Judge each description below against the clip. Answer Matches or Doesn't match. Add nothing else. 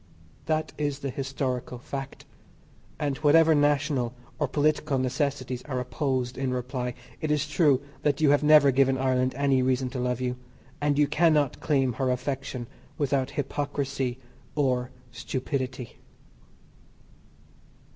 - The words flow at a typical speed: Doesn't match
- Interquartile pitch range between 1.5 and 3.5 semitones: Matches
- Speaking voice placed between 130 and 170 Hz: Matches